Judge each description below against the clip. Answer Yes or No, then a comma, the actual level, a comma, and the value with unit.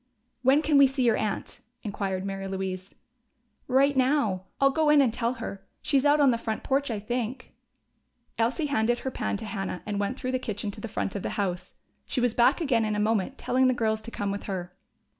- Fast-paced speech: Yes, fast, 220 wpm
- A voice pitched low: No, high, 230 Hz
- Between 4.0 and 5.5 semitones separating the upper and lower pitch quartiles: Yes, average, 4.7 semitones